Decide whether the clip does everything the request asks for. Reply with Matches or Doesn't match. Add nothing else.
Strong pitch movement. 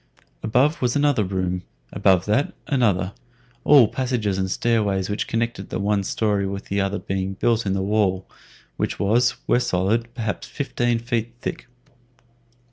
Doesn't match